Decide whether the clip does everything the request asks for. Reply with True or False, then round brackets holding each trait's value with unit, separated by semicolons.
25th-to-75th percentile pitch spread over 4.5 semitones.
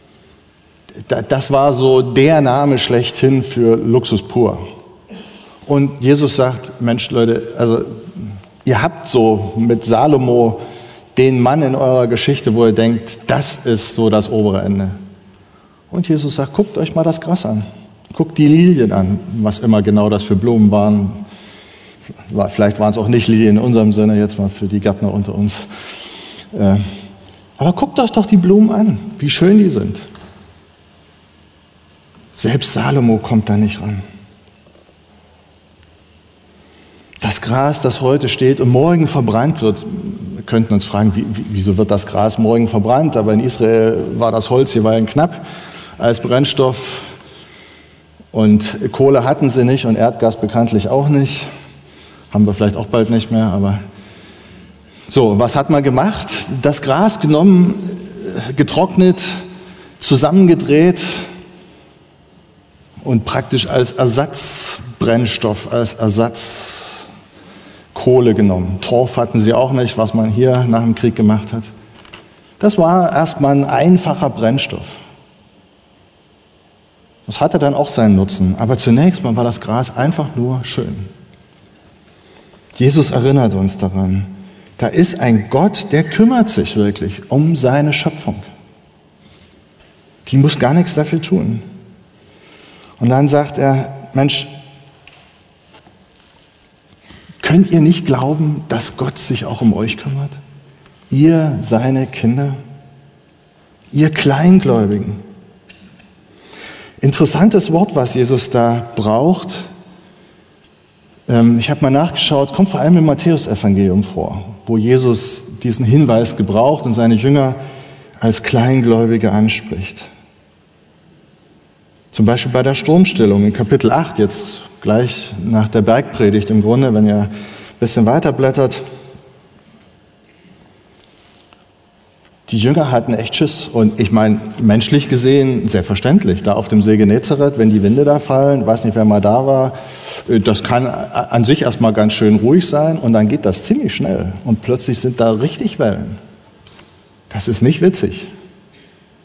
True (5.1 semitones)